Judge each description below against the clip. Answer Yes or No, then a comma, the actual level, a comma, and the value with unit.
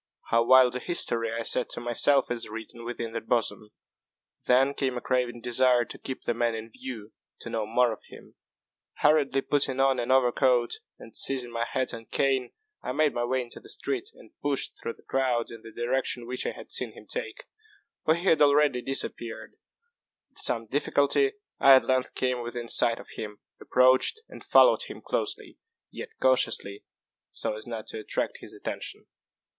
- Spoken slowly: No, average, 185 wpm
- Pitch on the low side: Yes, low, 125 Hz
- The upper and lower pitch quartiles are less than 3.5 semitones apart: Yes, narrow, 2.4 semitones